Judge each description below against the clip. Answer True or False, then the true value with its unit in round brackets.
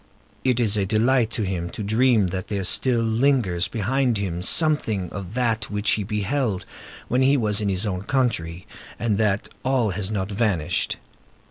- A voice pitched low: True (105 Hz)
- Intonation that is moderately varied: True (4.0 semitones)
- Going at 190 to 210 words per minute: False (170 wpm)